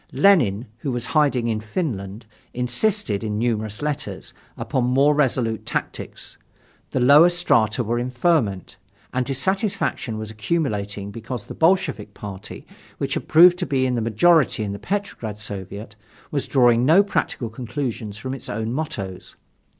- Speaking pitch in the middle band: No, low, 120 Hz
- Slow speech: No, average, 150 wpm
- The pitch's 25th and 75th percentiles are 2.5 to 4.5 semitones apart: No, wide, 5.6 semitones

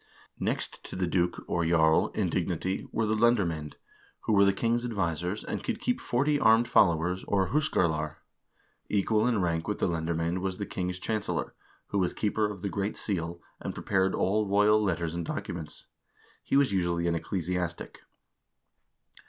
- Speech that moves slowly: No, average, 165 wpm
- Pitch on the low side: Yes, very low, 95 Hz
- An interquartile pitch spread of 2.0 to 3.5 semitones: No, average, 3.9 semitones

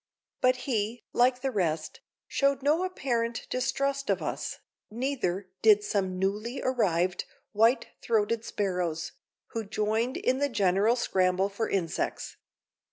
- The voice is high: Yes, high, 220 Hz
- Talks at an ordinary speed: No, slow, 125 wpm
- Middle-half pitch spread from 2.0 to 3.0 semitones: No, average, 4.7 semitones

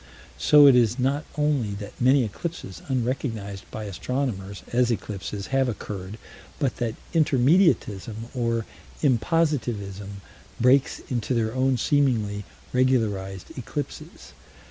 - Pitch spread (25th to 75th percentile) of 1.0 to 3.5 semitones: No, average, 4.7 semitones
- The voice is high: No, low, 120 Hz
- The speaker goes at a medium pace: No, slow, 110 wpm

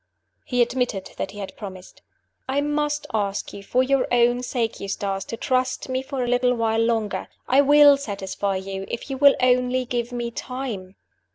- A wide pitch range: No, average, 4.1 semitones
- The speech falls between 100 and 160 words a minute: No, average, 180 wpm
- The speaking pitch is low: No, high, 245 Hz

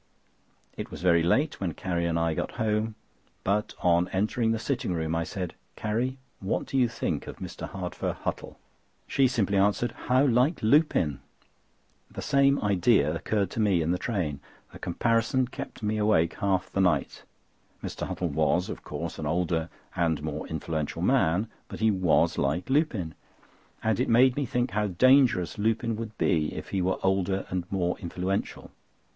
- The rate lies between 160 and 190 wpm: Yes, average, 170 wpm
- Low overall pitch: Yes, low, 100 Hz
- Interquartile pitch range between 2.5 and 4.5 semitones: No, average, 5.0 semitones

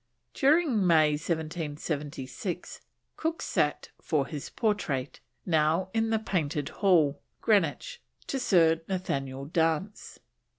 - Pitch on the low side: No, medium, 165 Hz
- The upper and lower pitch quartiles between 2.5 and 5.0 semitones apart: No, wide, 5.4 semitones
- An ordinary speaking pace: No, slow, 100 wpm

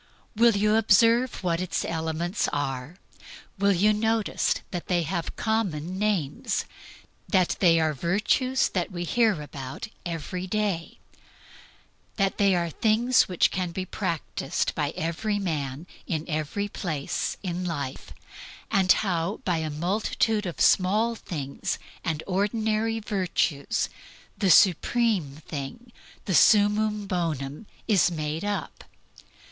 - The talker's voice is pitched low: No, medium, 185 Hz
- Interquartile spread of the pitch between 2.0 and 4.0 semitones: No, average, 4.7 semitones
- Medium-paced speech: No, slow, 125 wpm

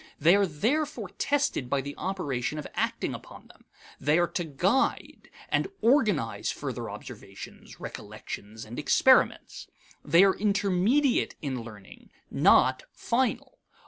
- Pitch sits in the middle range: Yes, medium, 180 Hz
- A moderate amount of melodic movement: No, wide, 8.7 semitones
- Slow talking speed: Yes, slow, 125 wpm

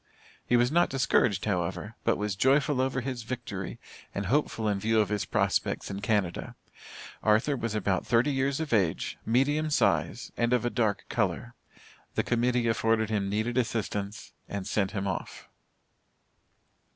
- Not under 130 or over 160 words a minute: Yes, average, 155 wpm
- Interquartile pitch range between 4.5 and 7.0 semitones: No, average, 3.9 semitones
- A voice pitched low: Yes, low, 110 Hz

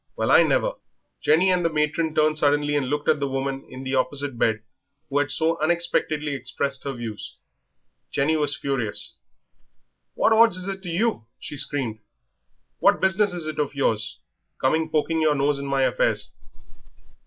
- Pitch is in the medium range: Yes, medium, 145 Hz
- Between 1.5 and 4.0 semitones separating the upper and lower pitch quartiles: Yes, average, 3.1 semitones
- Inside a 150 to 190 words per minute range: Yes, average, 170 wpm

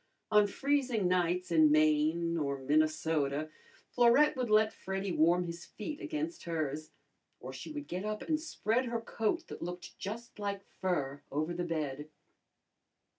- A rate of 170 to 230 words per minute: No, average, 150 wpm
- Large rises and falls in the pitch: Yes, wide, 6.6 semitones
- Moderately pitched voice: Yes, medium, 180 Hz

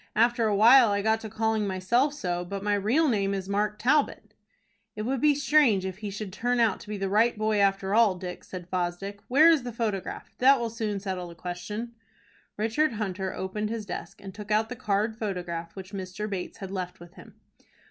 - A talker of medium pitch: No, high, 210 Hz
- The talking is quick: Yes, fast, 210 wpm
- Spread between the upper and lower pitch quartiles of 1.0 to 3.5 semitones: Yes, average, 3.1 semitones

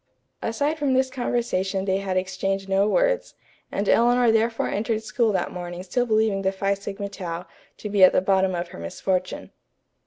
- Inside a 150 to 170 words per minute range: No, average, 180 wpm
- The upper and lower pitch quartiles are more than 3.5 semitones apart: No, average, 3.2 semitones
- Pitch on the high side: Yes, high, 200 Hz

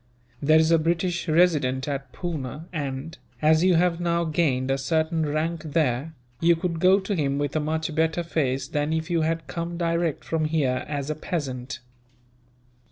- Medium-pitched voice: Yes, medium, 160 Hz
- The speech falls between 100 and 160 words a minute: No, average, 175 wpm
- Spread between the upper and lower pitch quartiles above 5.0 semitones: No, average, 2.7 semitones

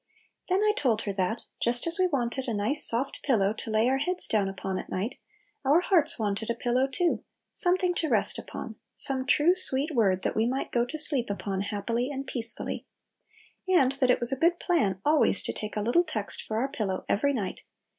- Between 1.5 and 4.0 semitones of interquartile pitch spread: No, wide, 5.4 semitones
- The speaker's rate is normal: No, fast, 210 wpm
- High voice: Yes, very high, 250 Hz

